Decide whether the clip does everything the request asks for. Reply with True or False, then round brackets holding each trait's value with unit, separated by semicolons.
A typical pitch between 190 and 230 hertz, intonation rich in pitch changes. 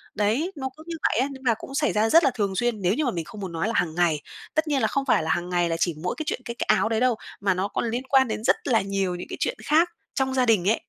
True (225 Hz; 6.1 semitones)